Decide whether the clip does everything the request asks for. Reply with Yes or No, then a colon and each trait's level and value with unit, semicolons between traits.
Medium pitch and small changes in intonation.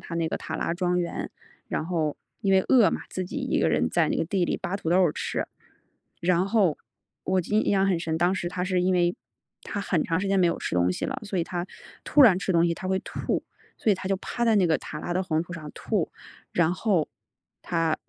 Yes: medium, 180 Hz; narrow, 2.3 semitones